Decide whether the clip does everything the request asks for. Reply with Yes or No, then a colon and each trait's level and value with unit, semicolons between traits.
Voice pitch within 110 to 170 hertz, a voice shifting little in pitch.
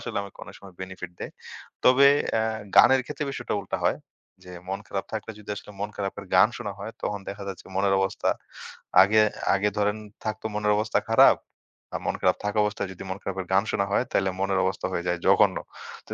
No: low, 100 Hz; narrow, 1.7 semitones